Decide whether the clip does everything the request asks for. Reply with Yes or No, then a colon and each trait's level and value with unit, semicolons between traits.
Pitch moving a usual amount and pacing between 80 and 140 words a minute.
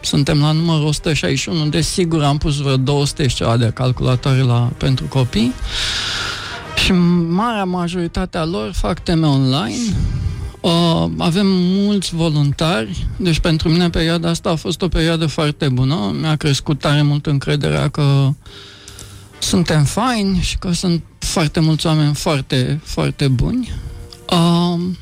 Yes: average, 4.0 semitones; average, 135 wpm